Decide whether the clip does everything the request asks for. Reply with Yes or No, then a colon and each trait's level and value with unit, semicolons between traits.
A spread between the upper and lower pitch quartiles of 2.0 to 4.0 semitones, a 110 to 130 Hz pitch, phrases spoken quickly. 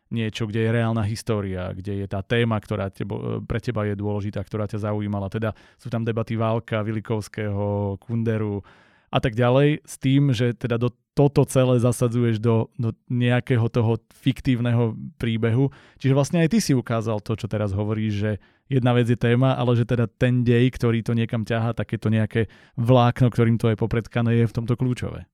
Yes: narrow, 2.4 semitones; low, 115 Hz; fast, 180 wpm